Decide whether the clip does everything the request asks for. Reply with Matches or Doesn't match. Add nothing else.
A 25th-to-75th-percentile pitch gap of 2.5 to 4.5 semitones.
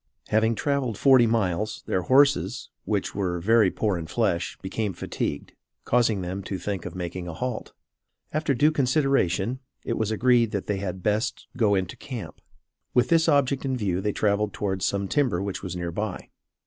Doesn't match